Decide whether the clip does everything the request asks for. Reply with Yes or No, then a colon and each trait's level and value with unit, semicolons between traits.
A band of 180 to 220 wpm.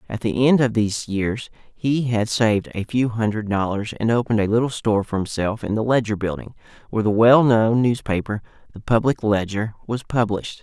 Yes: average, 185 wpm